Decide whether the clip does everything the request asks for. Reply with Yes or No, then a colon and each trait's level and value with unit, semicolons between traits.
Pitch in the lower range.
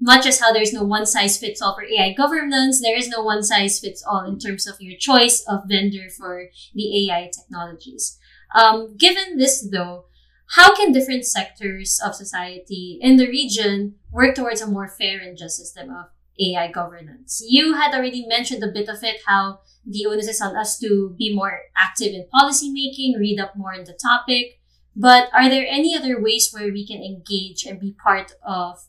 No: high, 210 Hz